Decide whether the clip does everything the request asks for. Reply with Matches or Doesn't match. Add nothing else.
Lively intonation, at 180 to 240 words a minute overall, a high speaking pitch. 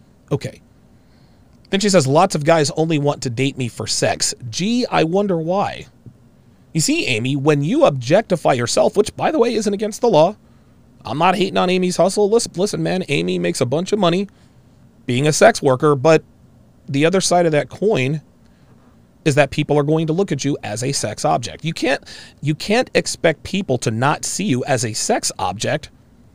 Doesn't match